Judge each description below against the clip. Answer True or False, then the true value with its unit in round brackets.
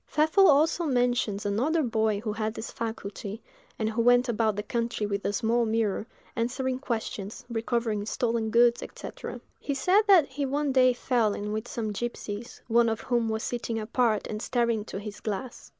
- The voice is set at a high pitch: True (230 Hz)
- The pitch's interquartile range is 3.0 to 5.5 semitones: False (2.6 semitones)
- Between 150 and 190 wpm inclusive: True (180 wpm)